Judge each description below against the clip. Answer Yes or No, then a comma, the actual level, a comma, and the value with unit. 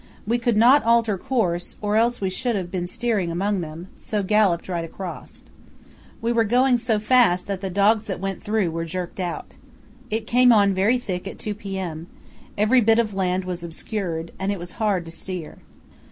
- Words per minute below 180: No, average, 195 wpm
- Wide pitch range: No, average, 3.9 semitones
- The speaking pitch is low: No, high, 200 Hz